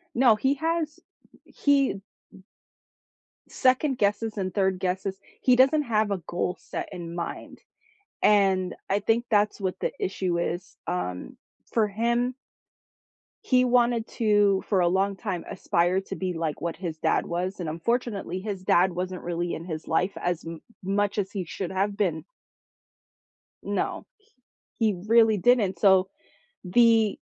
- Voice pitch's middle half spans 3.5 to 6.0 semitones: Yes, average, 4.2 semitones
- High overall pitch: Yes, high, 195 Hz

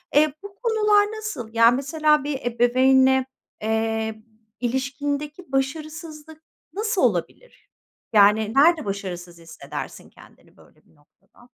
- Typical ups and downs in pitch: No, wide, 5.7 semitones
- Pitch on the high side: Yes, very high, 265 Hz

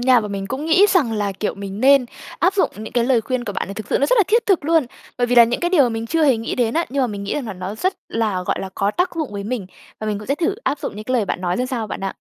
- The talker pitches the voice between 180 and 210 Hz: No, high, 240 Hz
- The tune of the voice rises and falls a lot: Yes, wide, 5.8 semitones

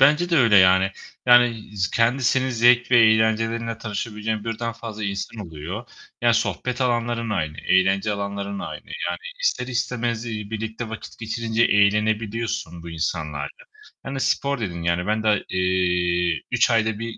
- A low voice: Yes, low, 110 Hz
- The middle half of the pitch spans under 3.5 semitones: Yes, average, 3.1 semitones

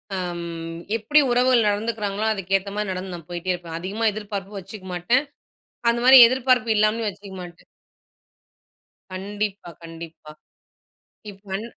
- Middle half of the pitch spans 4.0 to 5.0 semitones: No, average, 3.6 semitones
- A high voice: Yes, high, 200 Hz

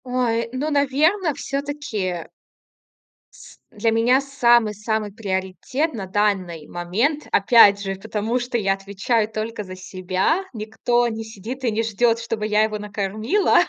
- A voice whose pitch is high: Yes, high, 220 Hz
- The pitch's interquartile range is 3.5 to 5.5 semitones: Yes, average, 3.8 semitones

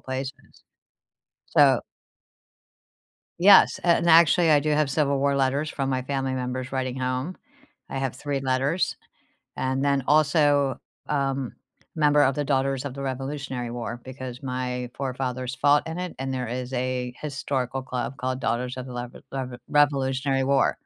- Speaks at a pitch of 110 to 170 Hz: Yes, low, 135 Hz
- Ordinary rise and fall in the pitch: No, narrow, 1.9 semitones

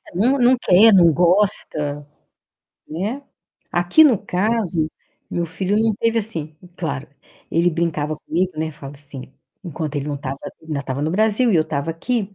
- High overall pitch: No, medium, 170 Hz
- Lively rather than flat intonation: Yes, wide, 5.7 semitones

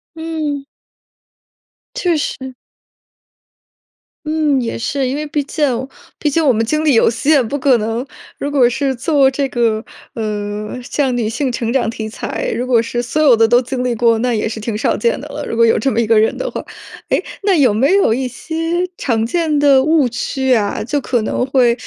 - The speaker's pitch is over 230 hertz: Yes, very high, 255 Hz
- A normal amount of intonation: Yes, average, 4.0 semitones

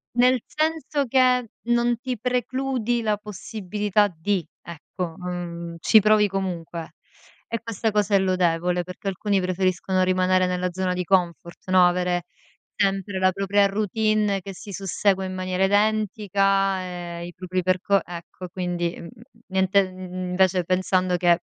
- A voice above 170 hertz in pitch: Yes, high, 190 Hz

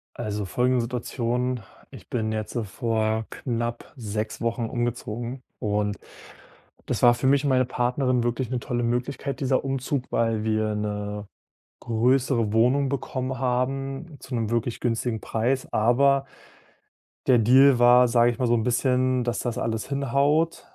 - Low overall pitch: Yes, low, 120 Hz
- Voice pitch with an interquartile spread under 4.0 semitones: Yes, narrow, 2.4 semitones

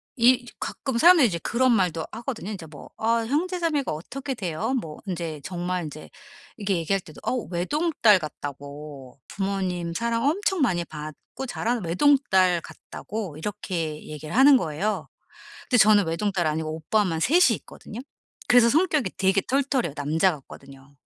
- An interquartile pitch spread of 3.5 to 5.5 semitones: No, wide, 7.3 semitones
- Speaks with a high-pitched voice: Yes, high, 195 Hz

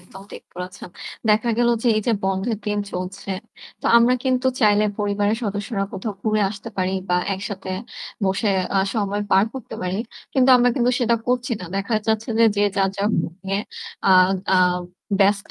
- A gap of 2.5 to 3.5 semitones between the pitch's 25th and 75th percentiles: Yes, average, 3.1 semitones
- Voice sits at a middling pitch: No, high, 205 Hz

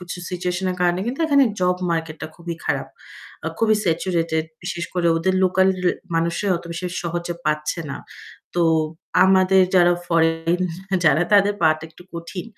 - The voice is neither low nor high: Yes, medium, 175 Hz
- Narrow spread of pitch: Yes, narrow, 2.0 semitones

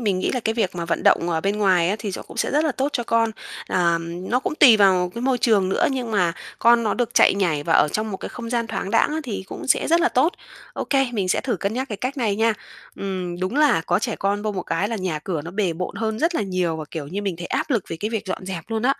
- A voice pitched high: Yes, high, 205 Hz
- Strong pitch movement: No, average, 4.5 semitones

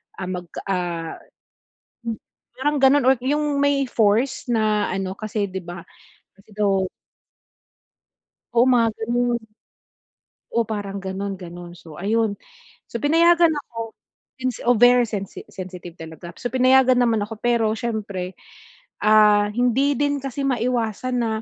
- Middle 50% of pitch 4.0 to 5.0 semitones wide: Yes, average, 4.4 semitones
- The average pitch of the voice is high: Yes, high, 225 Hz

